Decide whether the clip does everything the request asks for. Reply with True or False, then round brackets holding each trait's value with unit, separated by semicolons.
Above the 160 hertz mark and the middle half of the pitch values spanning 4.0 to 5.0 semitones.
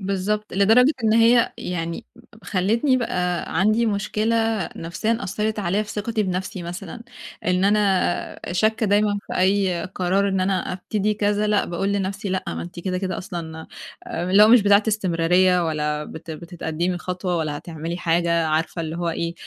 False (190 Hz; 3.5 semitones)